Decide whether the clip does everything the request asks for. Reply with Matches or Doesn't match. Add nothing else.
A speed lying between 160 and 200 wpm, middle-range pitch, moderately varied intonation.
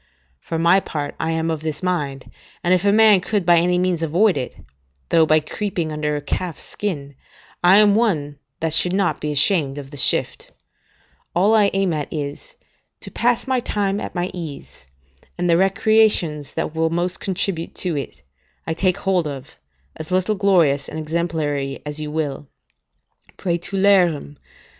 Matches